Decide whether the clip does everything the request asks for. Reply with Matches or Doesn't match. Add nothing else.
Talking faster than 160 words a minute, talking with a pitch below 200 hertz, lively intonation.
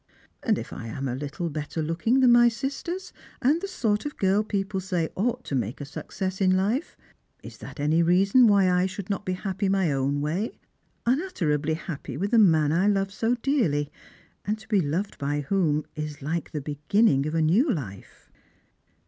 Matches